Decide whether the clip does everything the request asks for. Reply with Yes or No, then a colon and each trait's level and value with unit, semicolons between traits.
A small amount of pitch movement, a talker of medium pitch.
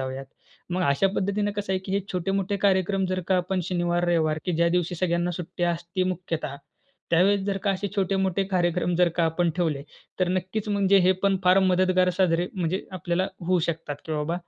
Yes: narrow, 1.9 semitones; medium, 180 Hz